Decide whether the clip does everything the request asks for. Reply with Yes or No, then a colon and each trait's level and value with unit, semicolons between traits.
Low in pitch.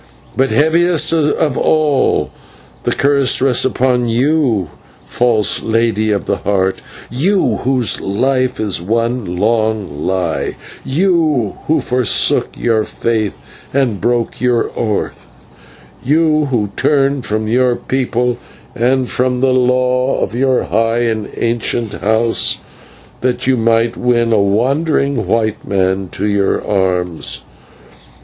Yes: low, 120 Hz